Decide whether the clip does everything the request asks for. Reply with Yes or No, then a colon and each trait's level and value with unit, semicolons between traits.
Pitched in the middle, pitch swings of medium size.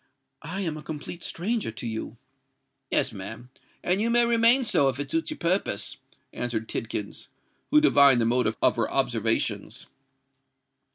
No: medium, 150 Hz; wide, 8.9 semitones